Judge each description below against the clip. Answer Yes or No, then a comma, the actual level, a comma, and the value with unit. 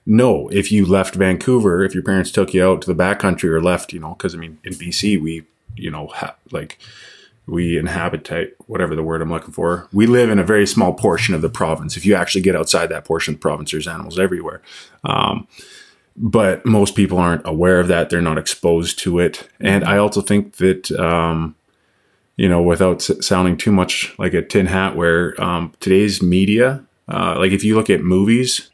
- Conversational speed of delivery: No, fast, 215 wpm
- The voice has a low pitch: Yes, very low, 95 Hz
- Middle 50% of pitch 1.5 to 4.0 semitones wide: Yes, average, 2.9 semitones